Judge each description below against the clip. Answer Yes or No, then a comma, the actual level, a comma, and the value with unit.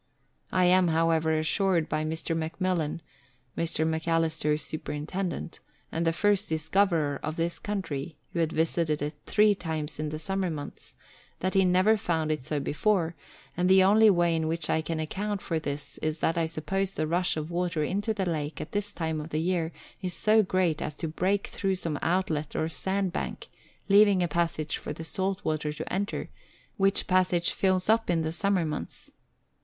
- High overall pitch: No, medium, 170 Hz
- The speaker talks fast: No, average, 185 wpm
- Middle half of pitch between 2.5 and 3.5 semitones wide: Yes, average, 3.2 semitones